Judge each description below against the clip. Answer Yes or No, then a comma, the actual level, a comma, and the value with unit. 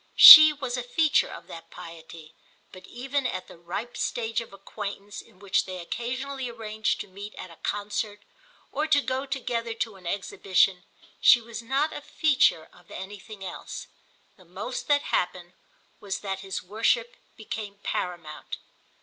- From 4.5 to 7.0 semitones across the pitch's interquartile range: Yes, average, 4.8 semitones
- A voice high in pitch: Yes, high, 210 Hz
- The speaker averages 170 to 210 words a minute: No, average, 160 wpm